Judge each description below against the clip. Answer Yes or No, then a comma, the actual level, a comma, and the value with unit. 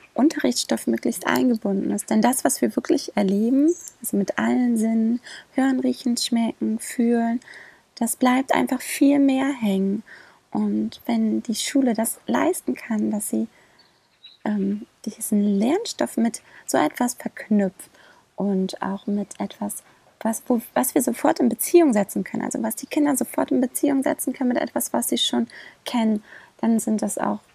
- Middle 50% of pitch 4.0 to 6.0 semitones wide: Yes, average, 4.4 semitones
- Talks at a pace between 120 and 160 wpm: Yes, average, 155 wpm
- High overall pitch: Yes, high, 235 Hz